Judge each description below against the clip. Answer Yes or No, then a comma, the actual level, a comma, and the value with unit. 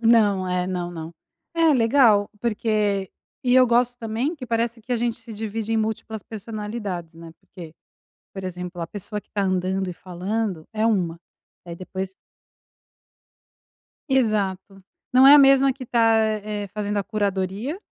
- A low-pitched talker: No, high, 210 Hz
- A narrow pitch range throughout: No, average, 3.7 semitones